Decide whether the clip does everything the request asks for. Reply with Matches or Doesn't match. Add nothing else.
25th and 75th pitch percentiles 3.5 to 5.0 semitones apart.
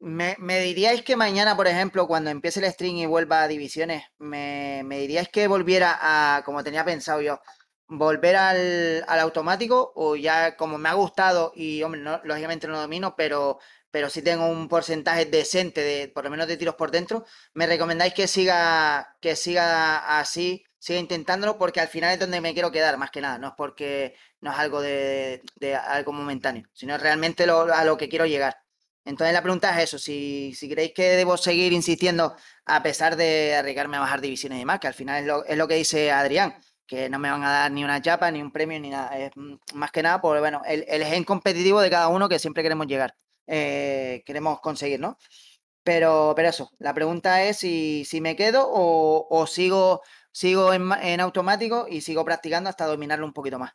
Doesn't match